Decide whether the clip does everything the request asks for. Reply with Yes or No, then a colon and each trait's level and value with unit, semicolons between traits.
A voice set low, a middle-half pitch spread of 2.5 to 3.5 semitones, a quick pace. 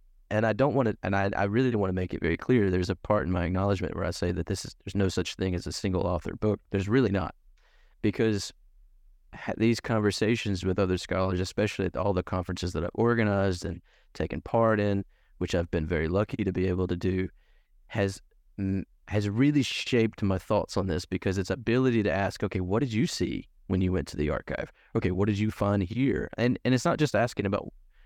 Yes: low, 100 Hz; average, 3.1 semitones; fast, 225 wpm